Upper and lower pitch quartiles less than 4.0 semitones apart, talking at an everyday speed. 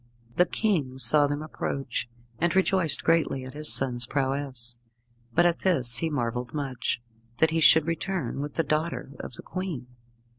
No: average, 4.3 semitones; average, 160 wpm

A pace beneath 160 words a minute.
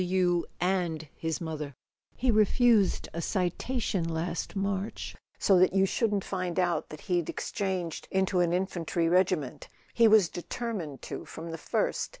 Yes: average, 150 wpm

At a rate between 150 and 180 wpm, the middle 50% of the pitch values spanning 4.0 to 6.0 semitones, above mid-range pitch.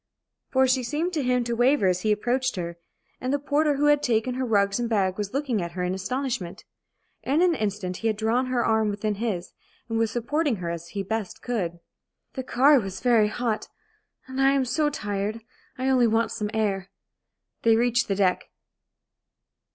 No: average, 195 wpm; average, 4.3 semitones; high, 230 Hz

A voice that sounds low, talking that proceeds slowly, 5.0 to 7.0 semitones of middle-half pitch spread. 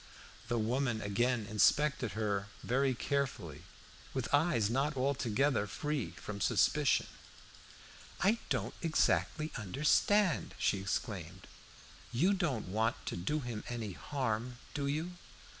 Yes: low, 125 Hz; slow, 115 wpm; average, 5.3 semitones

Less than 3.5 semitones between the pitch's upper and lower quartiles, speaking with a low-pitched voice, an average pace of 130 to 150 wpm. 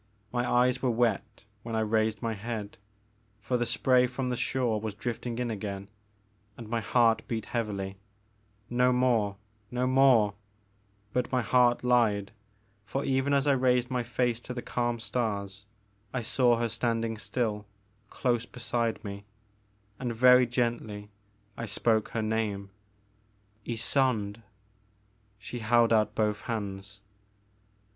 Yes: average, 2.9 semitones; low, 115 Hz; average, 145 wpm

